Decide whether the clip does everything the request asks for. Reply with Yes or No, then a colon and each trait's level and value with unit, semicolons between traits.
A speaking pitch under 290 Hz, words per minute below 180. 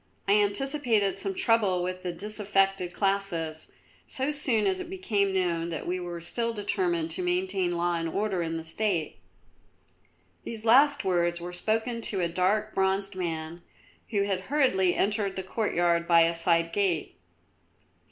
Yes: high, 190 Hz; average, 155 wpm